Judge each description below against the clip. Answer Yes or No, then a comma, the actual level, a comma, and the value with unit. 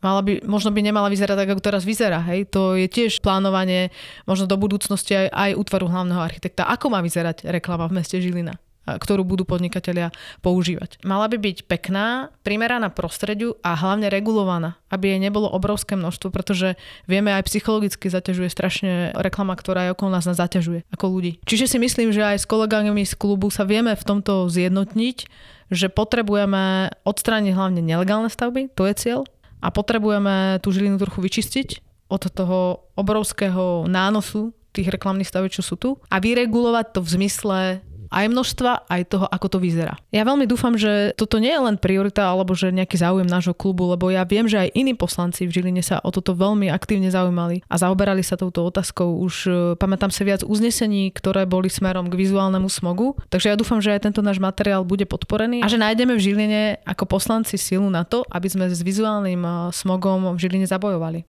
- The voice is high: Yes, high, 195 Hz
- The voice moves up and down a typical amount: No, narrow, 2.3 semitones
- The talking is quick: Yes, fast, 185 wpm